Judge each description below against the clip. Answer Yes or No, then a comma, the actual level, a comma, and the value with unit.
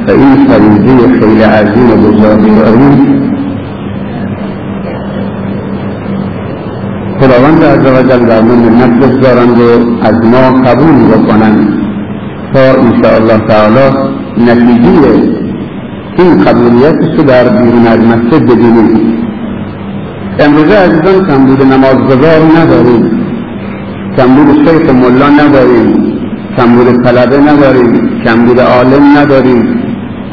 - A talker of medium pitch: No, low, 125 Hz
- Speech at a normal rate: No, slow, 100 wpm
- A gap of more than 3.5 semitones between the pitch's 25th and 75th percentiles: No, average, 3.0 semitones